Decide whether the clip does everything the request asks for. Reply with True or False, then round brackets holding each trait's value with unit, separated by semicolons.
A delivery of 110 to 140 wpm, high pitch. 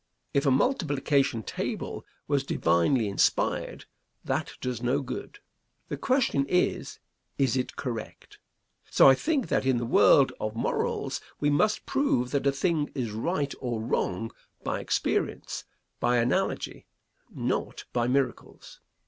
False (135 wpm; 135 Hz)